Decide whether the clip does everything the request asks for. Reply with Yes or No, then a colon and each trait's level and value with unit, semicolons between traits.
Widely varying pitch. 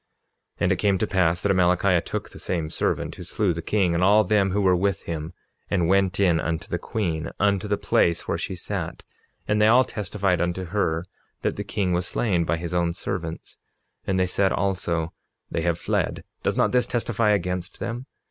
No: average, 3.0 semitones